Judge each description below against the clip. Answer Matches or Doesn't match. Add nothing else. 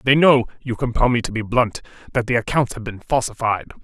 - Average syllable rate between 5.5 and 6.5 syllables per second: Matches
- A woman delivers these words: Doesn't match